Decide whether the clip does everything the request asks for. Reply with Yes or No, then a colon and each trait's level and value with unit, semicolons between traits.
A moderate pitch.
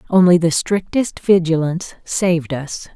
Yes: medium, 175 Hz